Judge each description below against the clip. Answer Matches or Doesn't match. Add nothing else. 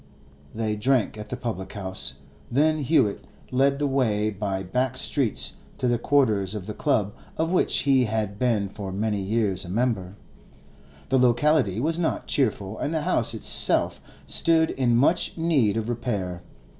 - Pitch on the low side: Matches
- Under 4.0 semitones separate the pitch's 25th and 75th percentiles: Doesn't match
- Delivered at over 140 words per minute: Matches